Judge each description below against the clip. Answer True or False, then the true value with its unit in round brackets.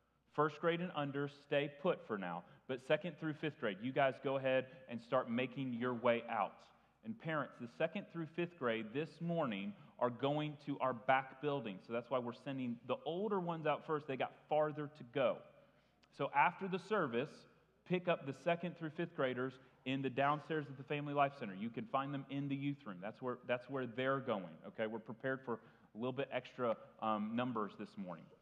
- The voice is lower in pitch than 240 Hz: True (140 Hz)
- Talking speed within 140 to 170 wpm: False (205 wpm)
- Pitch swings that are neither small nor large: True (3.6 semitones)